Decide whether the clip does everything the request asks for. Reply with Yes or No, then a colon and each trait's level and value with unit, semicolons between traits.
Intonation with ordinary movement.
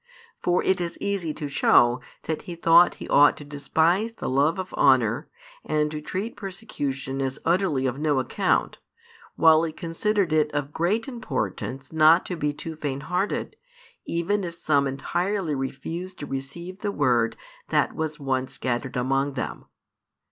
Yes: average, 4.6 semitones